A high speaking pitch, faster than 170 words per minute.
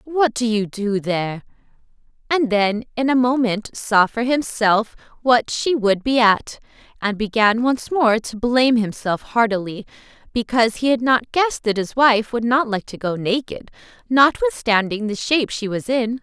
No: high, 230 Hz; average, 165 wpm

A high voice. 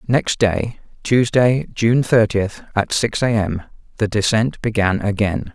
No: low, 110 Hz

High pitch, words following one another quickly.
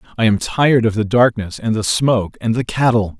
No: low, 110 Hz; fast, 225 wpm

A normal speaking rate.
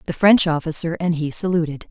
Yes: average, 190 wpm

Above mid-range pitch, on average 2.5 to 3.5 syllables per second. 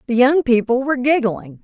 No: very high, 250 Hz; 5.5 syllables/s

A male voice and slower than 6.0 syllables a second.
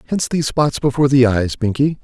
No: male; 6.6 syllables/s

